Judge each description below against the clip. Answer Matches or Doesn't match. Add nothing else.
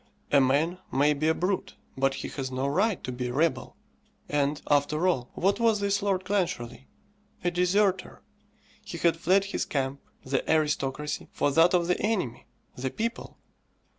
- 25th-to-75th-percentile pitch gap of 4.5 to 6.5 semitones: Matches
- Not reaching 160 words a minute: Doesn't match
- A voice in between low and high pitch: Matches